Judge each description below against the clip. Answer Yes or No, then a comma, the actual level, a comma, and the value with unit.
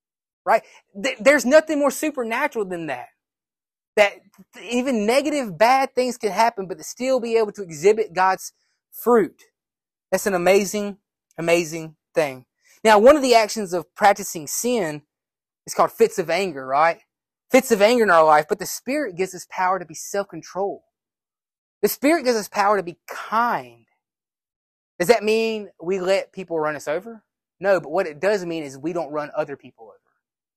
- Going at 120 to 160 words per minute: No, average, 175 wpm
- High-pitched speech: Yes, high, 200 Hz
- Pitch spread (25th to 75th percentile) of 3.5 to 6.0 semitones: Yes, average, 5.1 semitones